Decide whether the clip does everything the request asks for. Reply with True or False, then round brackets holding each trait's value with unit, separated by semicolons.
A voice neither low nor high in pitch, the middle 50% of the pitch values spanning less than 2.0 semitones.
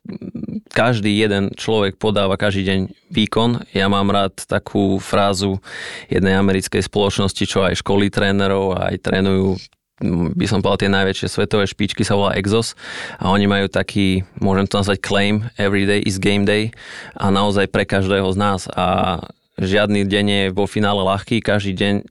False (100 Hz; 1.2 semitones)